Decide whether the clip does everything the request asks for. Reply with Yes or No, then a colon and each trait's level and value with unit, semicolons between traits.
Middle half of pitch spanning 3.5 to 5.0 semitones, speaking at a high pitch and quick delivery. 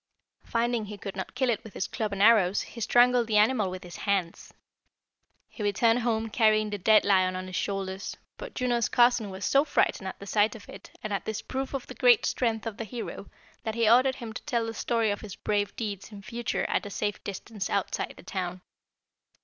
No: average, 2.8 semitones; high, 215 Hz; fast, 220 wpm